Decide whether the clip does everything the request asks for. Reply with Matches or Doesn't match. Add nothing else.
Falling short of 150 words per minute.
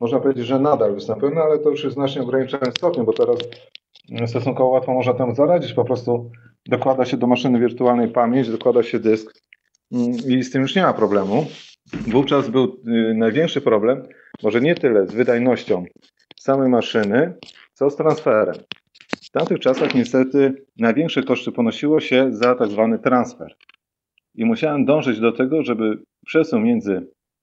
Doesn't match